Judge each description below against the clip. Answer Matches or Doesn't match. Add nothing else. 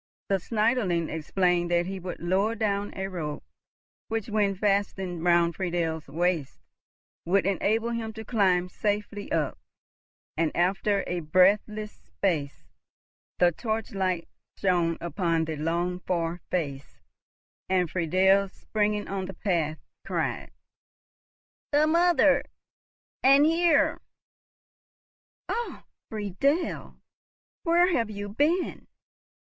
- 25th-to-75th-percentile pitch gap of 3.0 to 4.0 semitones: Matches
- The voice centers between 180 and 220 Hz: Matches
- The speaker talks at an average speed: Doesn't match